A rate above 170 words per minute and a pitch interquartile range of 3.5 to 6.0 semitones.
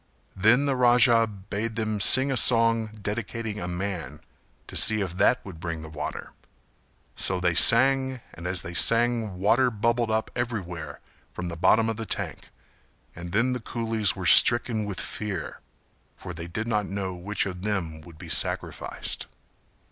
No: average, 165 wpm; average, 4.4 semitones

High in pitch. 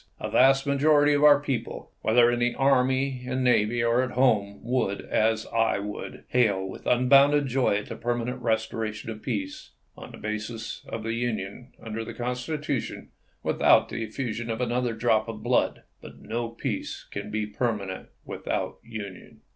No: low, 120 Hz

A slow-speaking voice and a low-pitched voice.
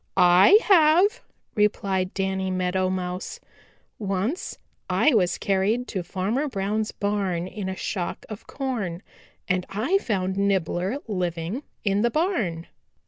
No: slow, 125 wpm; high, 195 Hz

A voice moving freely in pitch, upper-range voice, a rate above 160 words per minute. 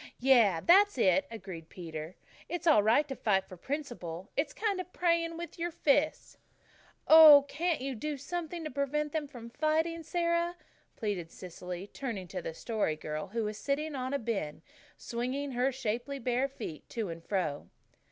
Yes: wide, 7.8 semitones; very high, 265 Hz; average, 170 wpm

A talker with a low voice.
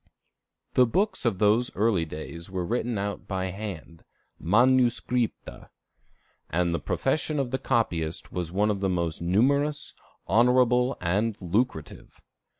Yes: low, 105 Hz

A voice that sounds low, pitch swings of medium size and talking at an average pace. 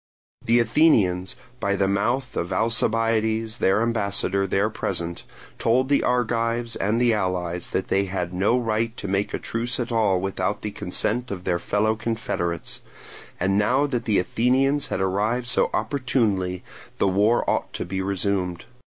Yes: low, 105 Hz; average, 3.6 semitones; average, 160 wpm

